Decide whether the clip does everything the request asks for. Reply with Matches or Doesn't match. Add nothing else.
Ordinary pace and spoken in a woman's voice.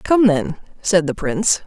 Matches